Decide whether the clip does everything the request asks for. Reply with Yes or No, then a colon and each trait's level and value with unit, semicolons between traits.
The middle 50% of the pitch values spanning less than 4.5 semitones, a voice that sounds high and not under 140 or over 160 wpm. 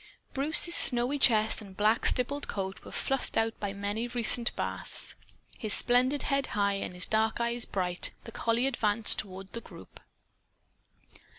Yes: average, 3.4 semitones; high, 225 Hz; average, 155 wpm